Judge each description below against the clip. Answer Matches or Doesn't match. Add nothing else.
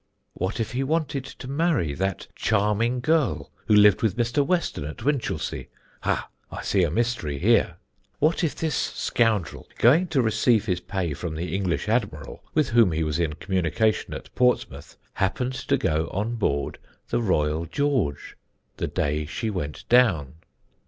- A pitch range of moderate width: Doesn't match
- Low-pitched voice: Matches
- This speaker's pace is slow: Doesn't match